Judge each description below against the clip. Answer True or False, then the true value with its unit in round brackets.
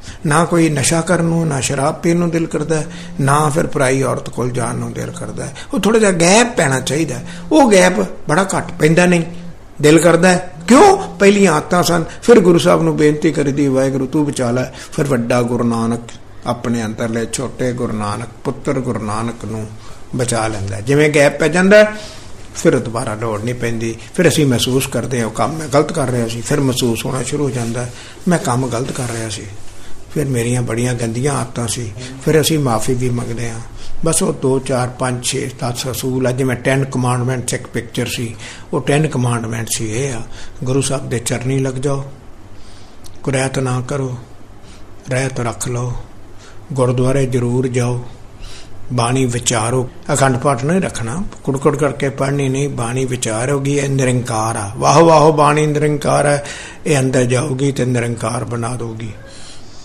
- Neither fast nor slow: False (170 wpm)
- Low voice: True (130 Hz)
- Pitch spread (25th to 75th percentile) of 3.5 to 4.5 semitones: True (4.1 semitones)